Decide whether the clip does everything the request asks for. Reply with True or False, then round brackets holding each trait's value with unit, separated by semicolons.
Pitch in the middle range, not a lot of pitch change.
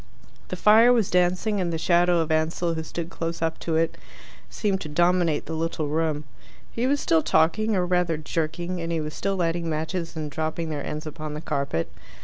True (165 Hz; 2.2 semitones)